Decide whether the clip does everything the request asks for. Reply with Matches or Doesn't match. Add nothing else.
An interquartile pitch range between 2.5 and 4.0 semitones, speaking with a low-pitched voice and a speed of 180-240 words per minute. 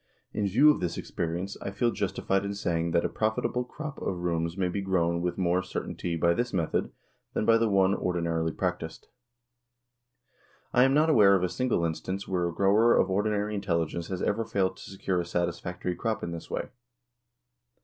Matches